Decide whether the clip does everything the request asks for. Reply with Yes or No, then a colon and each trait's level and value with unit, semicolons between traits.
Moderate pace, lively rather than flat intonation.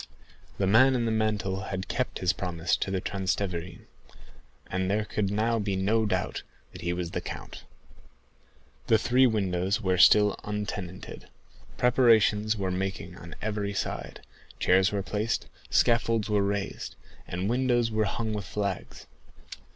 No: average, 145 wpm; average, 2.8 semitones